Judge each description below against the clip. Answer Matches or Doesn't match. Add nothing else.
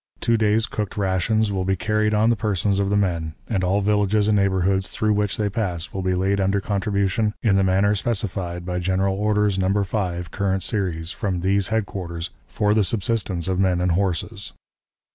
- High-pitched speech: Doesn't match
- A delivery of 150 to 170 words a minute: Doesn't match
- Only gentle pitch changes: Matches